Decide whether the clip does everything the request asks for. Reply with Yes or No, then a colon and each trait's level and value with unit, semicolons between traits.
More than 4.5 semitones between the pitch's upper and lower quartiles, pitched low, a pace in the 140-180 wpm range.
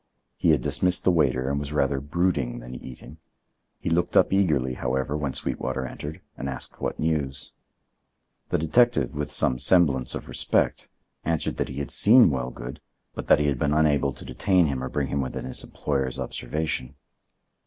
No: average, 3.4 semitones; very low, 70 Hz; average, 175 wpm